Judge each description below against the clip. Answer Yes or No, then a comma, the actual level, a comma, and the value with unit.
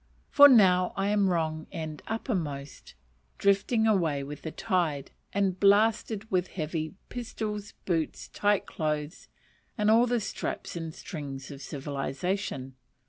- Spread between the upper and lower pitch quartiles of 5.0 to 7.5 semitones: Yes, average, 5.3 semitones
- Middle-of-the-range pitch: Yes, medium, 180 Hz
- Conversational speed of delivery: No, slow, 130 wpm